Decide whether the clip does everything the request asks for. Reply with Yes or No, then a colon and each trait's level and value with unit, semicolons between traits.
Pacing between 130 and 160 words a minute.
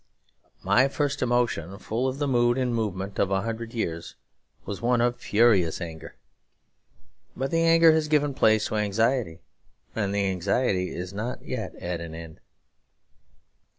Yes: average, 150 wpm